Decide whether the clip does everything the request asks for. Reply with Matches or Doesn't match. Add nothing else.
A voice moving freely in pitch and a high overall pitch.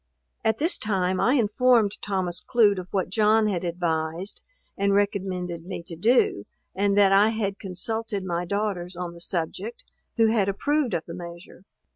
Doesn't match